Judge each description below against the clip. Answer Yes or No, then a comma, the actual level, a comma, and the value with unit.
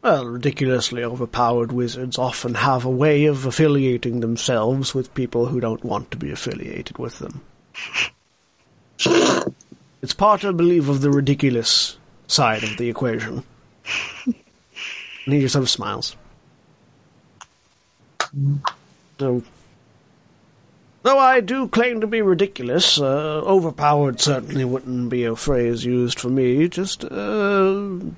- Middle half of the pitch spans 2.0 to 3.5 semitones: No, average, 4.6 semitones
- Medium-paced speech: No, slow, 120 wpm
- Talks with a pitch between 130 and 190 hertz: Yes, low, 135 Hz